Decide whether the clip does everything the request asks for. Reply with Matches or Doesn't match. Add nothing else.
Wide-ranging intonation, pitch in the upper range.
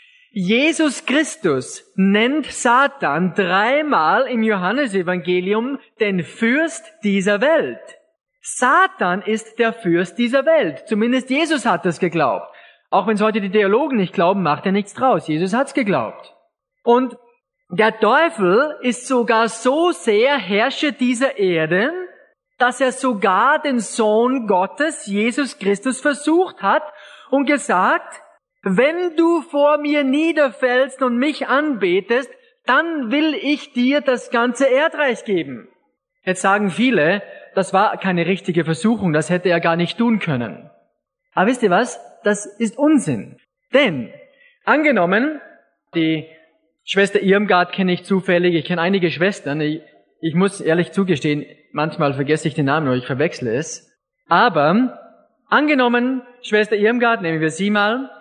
Matches